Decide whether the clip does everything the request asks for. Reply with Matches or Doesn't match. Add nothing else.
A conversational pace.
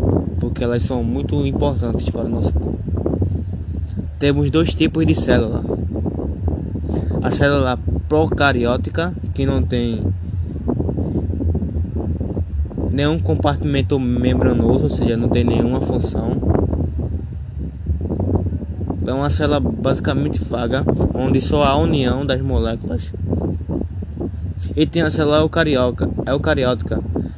Doesn't match